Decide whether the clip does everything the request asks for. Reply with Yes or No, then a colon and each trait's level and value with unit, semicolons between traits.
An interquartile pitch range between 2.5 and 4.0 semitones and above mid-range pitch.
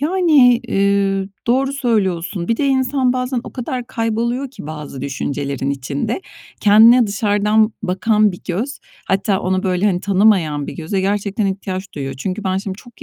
No: average, 4.5 semitones; high, 200 Hz